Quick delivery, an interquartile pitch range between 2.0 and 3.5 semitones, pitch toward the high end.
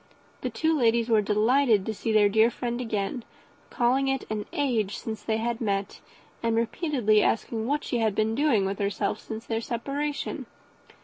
No: average, 175 wpm; narrow, 2.6 semitones; high, 225 Hz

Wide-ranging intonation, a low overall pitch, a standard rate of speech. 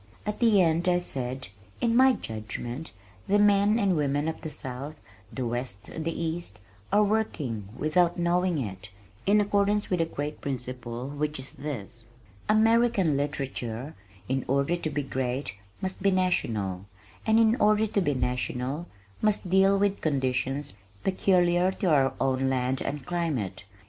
No: wide, 6.7 semitones; medium, 155 Hz; average, 155 wpm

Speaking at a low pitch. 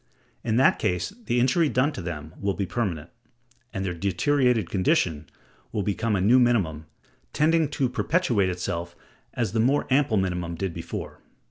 Yes: low, 100 Hz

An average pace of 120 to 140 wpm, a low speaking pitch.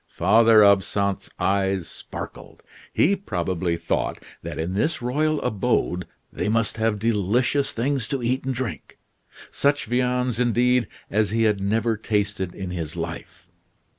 Yes: slow, 135 wpm; low, 110 Hz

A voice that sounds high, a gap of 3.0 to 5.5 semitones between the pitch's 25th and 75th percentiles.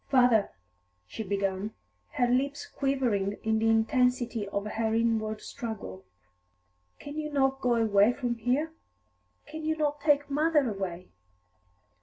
Yes: high, 235 Hz; average, 4.5 semitones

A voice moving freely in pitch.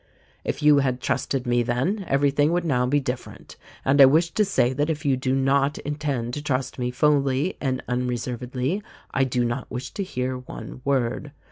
No: average, 2.7 semitones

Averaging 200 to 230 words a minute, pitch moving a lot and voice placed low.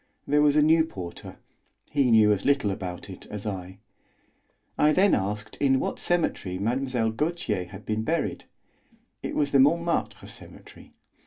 No: average, 155 wpm; wide, 6.6 semitones; low, 120 Hz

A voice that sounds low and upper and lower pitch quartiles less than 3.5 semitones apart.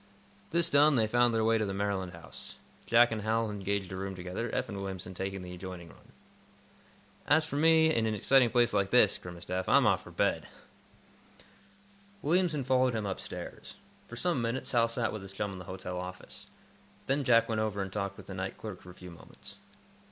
No: low, 105 Hz; average, 4.4 semitones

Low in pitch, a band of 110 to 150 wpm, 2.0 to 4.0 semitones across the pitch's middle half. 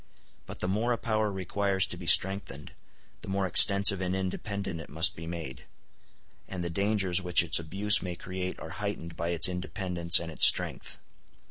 No: very low, 90 Hz; average, 175 wpm; narrow, 2.6 semitones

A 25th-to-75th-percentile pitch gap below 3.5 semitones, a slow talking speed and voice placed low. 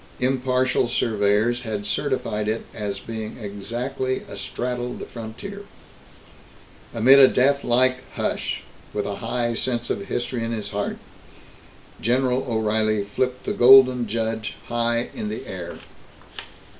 Yes: average, 2.8 semitones; slow, 120 wpm; low, 120 Hz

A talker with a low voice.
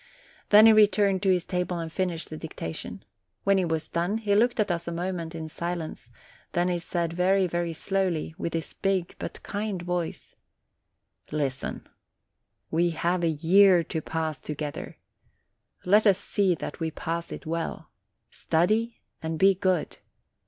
No: medium, 175 Hz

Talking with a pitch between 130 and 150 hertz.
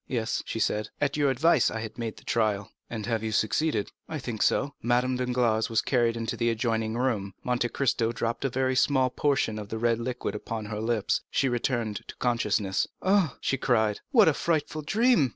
No: low, 120 Hz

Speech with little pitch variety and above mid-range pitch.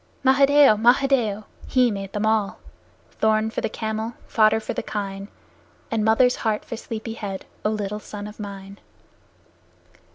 Yes: narrow, 1.9 semitones; high, 220 Hz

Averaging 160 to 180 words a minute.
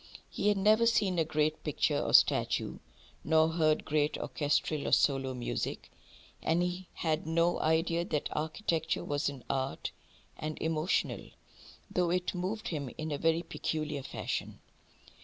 No: average, 145 wpm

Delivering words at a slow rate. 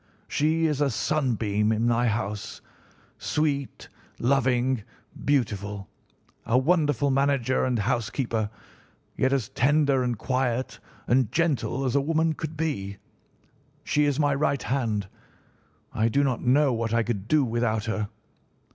Yes: slow, 130 wpm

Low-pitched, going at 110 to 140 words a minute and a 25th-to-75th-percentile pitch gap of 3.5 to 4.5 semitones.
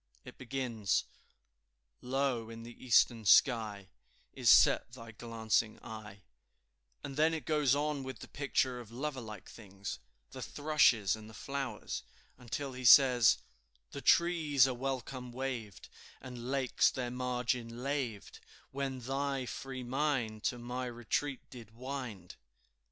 No: low, 125 Hz; slow, 135 wpm; average, 3.0 semitones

